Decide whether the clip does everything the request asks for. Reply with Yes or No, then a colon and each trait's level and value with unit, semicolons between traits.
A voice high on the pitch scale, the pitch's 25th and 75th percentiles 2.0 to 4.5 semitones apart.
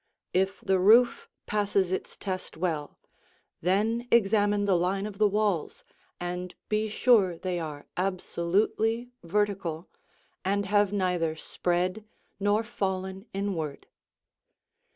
Yes: high, 195 Hz; narrow, 2.5 semitones